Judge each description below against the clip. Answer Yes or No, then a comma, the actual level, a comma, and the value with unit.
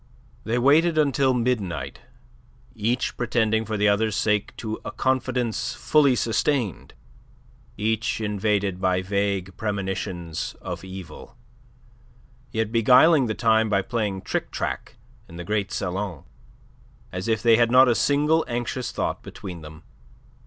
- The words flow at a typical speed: No, slow, 130 wpm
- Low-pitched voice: Yes, low, 110 Hz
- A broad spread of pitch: No, average, 3.8 semitones